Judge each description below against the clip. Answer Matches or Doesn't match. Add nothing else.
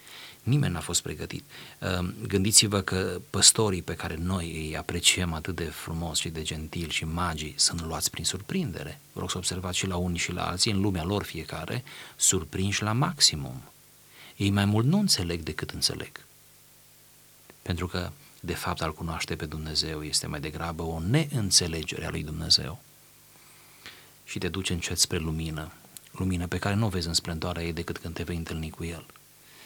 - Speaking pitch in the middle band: Doesn't match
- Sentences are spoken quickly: Matches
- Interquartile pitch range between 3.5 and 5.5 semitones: Doesn't match